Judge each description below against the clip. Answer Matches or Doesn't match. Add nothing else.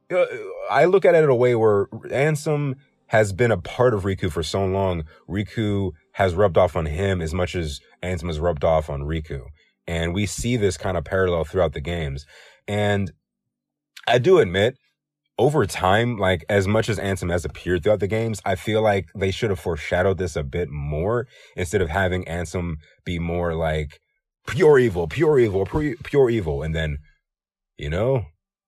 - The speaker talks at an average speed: Matches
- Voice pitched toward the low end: Matches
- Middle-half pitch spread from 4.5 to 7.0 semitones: Matches